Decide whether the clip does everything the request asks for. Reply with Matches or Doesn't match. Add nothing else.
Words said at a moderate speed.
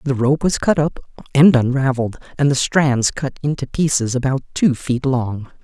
Matches